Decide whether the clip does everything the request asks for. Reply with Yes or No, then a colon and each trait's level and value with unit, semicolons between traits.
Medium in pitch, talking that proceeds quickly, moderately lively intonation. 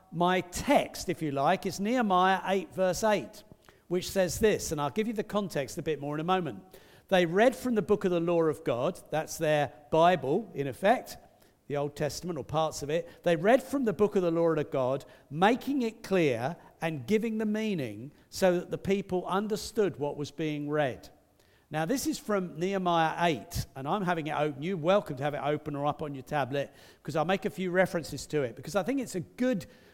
Yes: medium, 170 Hz; fast, 220 wpm; average, 4.7 semitones